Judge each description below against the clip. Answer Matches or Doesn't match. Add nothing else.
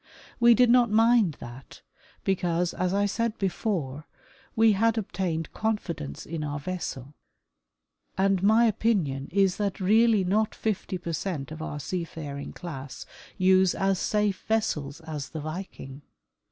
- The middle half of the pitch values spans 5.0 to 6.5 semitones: Matches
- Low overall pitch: Doesn't match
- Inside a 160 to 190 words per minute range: Doesn't match